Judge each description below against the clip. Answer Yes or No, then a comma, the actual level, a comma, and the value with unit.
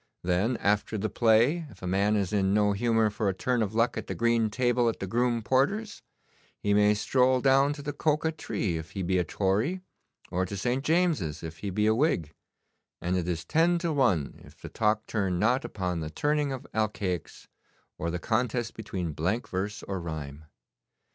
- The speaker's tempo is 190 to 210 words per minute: Yes, average, 200 wpm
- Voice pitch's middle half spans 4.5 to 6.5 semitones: Yes, average, 5.3 semitones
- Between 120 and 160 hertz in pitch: No, low, 110 Hz